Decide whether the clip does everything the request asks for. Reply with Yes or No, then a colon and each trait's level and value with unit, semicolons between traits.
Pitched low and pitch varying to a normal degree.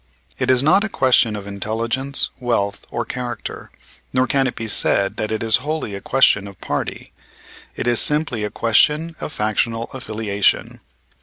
Yes: low, 115 Hz; average, 3.8 semitones